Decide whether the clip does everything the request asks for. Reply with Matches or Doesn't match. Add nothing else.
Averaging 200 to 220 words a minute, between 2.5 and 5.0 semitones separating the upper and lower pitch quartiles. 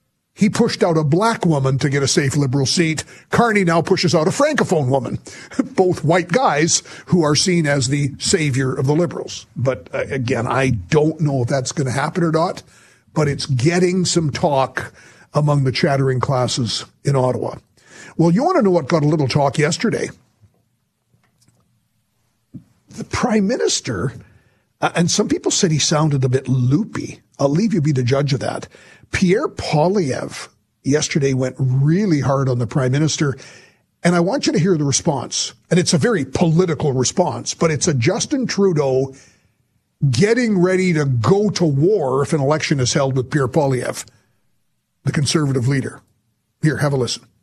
Doesn't match